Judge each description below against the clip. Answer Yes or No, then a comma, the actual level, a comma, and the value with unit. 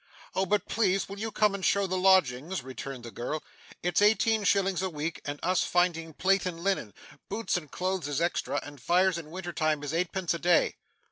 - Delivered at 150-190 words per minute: No, fast, 205 wpm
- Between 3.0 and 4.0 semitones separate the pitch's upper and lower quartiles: Yes, average, 3.6 semitones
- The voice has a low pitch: No, medium, 180 Hz